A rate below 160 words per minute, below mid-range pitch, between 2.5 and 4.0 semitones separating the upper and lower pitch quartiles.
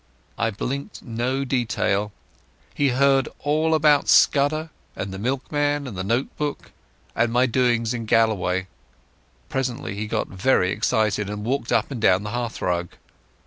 No: average, 145 wpm; low, 120 Hz; average, 4.6 semitones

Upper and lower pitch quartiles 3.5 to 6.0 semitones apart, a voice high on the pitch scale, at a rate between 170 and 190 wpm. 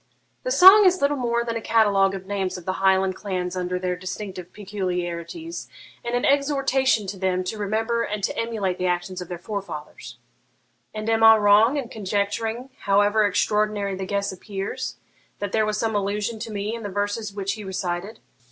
No: average, 2.9 semitones; high, 205 Hz; average, 185 wpm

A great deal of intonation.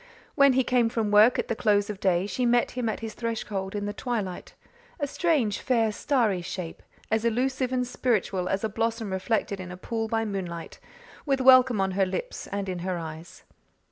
No: average, 4.2 semitones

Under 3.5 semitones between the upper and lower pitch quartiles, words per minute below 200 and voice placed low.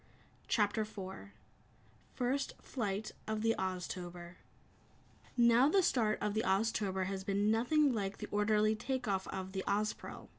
No: average, 2.9 semitones; average, 140 wpm; high, 210 Hz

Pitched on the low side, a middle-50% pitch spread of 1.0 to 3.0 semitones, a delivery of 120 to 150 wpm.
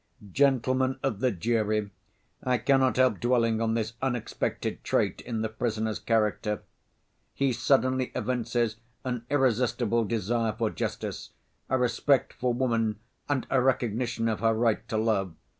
Yes: low, 120 Hz; narrow, 2.5 semitones; average, 140 wpm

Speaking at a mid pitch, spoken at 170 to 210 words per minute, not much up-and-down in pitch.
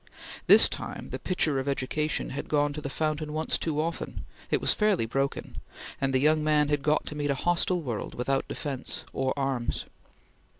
Yes: medium, 145 Hz; average, 185 wpm; narrow, 2.2 semitones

